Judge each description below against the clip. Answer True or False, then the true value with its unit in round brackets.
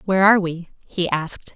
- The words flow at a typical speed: True (195 wpm)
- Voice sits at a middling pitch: True (180 Hz)